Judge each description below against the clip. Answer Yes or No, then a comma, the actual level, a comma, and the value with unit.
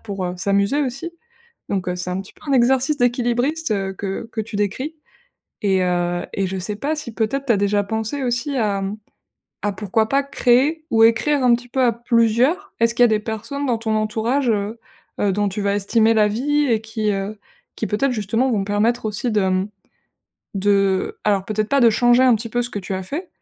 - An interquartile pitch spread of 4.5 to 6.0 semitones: No, average, 3.6 semitones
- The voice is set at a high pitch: Yes, high, 220 Hz